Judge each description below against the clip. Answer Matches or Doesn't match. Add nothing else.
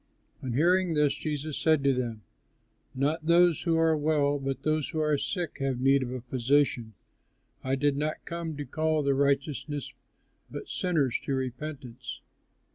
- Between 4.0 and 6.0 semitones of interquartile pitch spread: Doesn't match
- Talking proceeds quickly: Doesn't match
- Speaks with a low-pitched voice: Doesn't match